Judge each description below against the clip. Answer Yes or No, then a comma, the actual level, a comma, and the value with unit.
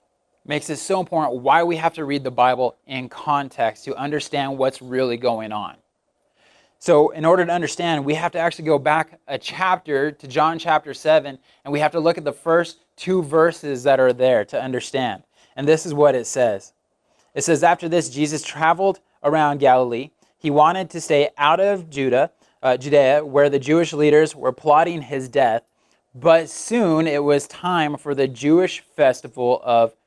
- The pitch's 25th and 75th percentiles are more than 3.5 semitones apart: No, average, 3.2 semitones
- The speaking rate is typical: Yes, average, 185 wpm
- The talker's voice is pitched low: No, medium, 150 Hz